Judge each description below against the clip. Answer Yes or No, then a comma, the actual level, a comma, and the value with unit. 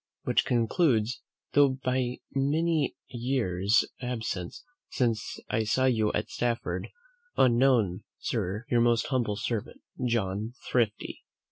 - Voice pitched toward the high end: No, low, 120 Hz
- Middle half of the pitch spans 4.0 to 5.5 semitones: No, average, 3.1 semitones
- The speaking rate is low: Yes, slow, 110 wpm